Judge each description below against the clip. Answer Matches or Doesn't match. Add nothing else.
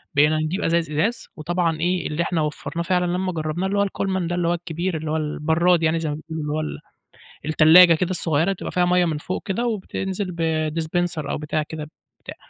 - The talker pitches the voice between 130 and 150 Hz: Doesn't match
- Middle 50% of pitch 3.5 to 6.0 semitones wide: Doesn't match